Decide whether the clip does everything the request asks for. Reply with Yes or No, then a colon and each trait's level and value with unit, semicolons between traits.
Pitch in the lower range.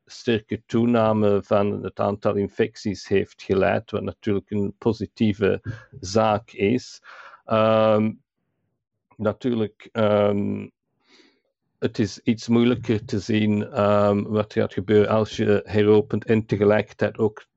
Yes: low, 105 Hz